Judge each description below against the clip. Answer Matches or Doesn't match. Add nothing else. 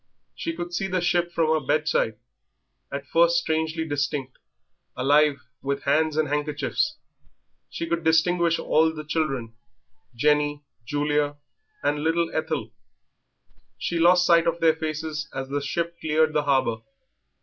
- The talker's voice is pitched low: Doesn't match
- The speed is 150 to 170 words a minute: Doesn't match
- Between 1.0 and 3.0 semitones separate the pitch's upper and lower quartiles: Matches